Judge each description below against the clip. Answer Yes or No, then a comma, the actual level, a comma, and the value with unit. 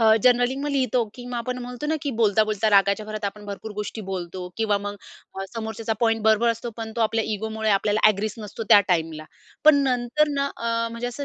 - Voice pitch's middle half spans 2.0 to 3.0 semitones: Yes, average, 2.7 semitones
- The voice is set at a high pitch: Yes, high, 220 Hz